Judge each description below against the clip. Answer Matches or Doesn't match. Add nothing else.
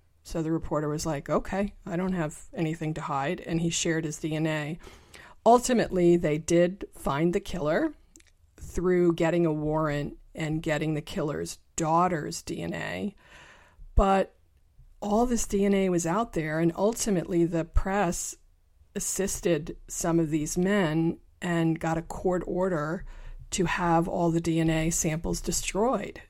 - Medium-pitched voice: Matches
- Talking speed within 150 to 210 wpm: Doesn't match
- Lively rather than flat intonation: Doesn't match